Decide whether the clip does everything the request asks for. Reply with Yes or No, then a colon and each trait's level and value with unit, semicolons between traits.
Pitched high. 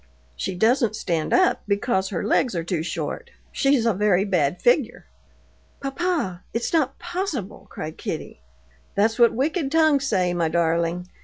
Yes: high, 215 Hz